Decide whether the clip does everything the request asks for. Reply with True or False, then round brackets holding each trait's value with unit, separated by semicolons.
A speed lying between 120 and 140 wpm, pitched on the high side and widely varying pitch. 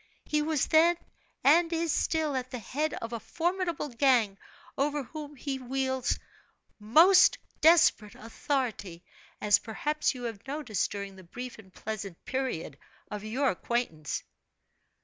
True (135 wpm; 260 Hz; 5.9 semitones)